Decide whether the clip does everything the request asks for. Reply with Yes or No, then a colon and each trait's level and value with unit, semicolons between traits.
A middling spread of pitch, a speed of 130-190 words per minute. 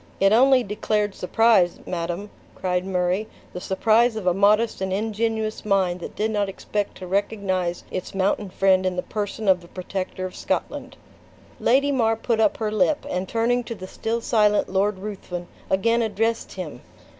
Yes: average, 3.1 semitones; average, 170 wpm